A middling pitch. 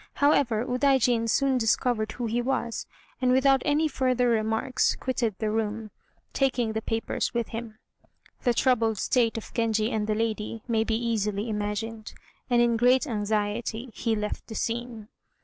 No: high, 230 Hz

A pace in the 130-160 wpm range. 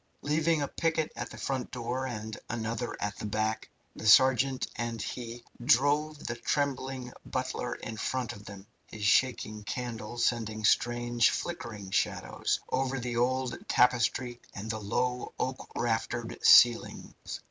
Yes: average, 140 wpm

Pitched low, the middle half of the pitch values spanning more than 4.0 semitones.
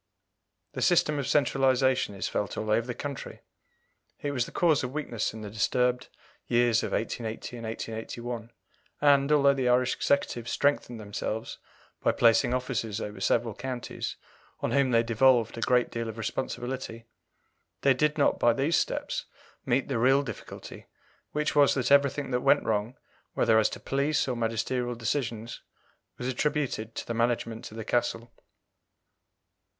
No: low, 125 Hz; average, 3.2 semitones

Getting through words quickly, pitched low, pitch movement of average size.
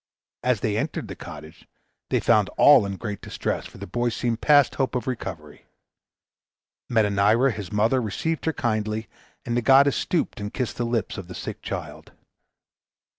No: average, 170 wpm; low, 115 Hz; average, 3.7 semitones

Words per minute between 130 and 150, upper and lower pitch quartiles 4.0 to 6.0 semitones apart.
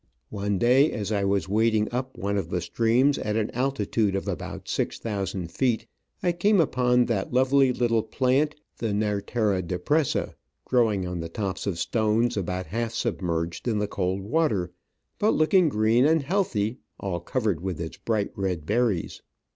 No: average, 165 wpm; average, 4.5 semitones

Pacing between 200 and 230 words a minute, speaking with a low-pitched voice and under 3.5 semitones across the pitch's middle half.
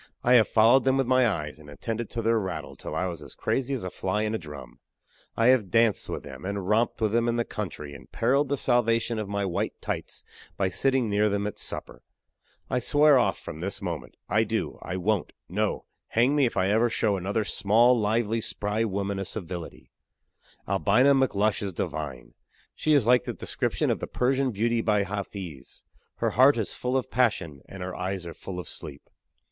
No: fast, 205 wpm; low, 105 Hz; average, 3.9 semitones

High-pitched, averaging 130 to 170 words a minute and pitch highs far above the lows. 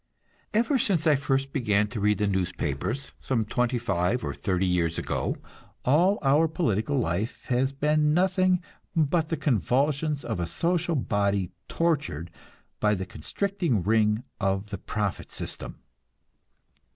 No: low, 125 Hz; average, 140 wpm; wide, 7.4 semitones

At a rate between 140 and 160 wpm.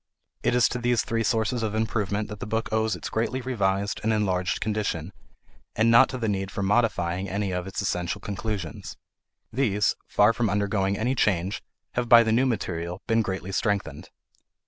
No: average, 180 wpm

